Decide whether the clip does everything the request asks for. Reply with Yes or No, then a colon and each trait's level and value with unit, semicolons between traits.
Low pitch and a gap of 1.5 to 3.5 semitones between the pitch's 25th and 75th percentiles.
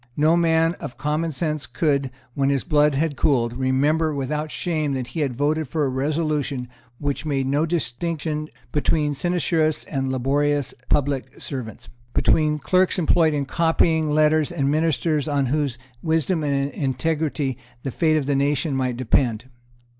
No: medium, 145 Hz; narrow, 2.6 semitones